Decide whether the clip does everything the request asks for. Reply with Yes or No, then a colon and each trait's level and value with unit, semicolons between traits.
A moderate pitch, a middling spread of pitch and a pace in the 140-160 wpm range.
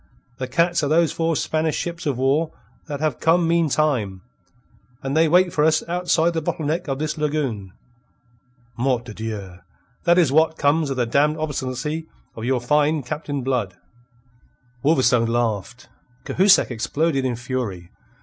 Yes: medium, 145 Hz; average, 4.5 semitones; average, 155 wpm